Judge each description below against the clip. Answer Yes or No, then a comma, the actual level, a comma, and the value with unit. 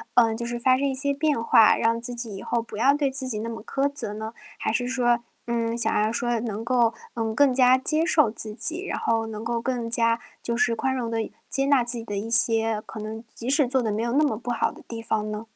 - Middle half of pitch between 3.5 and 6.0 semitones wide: No, narrow, 2.5 semitones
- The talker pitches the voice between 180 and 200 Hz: No, high, 235 Hz